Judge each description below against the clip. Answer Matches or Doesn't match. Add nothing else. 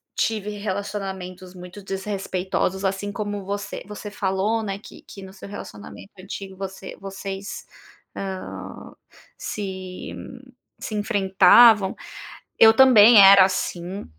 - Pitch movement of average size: Doesn't match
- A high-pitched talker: Matches